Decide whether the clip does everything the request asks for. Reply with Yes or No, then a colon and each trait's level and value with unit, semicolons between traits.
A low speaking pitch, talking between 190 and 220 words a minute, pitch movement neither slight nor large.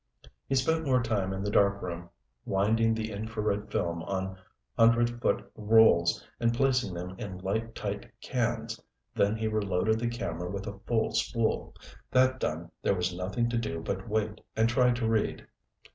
No: low, 110 Hz; average, 165 wpm; average, 3.4 semitones